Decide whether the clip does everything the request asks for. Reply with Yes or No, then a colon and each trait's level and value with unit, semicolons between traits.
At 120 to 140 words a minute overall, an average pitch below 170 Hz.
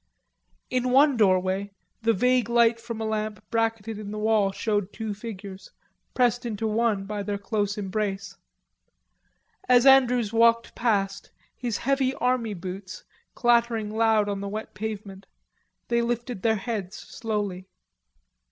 No: slow, 135 wpm; high, 220 Hz